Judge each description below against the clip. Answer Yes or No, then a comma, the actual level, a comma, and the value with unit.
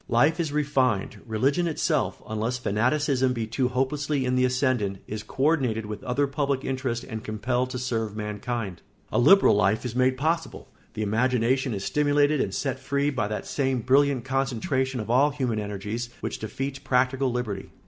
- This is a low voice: Yes, low, 125 Hz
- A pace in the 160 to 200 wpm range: Yes, average, 170 wpm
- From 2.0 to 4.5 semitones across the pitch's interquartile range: Yes, average, 3.6 semitones